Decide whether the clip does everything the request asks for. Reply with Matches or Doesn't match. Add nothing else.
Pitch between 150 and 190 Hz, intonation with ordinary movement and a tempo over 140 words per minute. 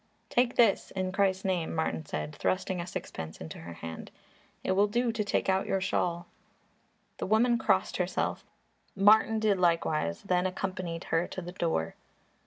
Matches